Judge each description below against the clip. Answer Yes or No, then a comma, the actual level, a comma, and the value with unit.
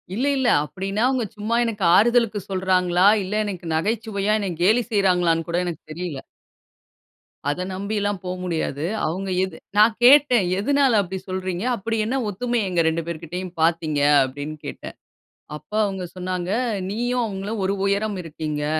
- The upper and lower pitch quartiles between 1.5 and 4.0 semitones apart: Yes, average, 3.7 semitones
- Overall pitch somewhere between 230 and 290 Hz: No, high, 190 Hz